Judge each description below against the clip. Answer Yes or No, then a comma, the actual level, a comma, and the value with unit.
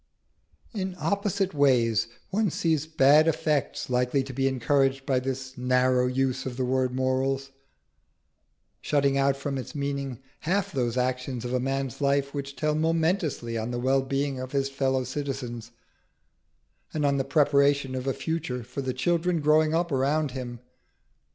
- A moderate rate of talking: Yes, average, 155 wpm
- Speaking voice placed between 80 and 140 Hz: Yes, low, 135 Hz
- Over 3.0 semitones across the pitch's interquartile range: No, average, 2.7 semitones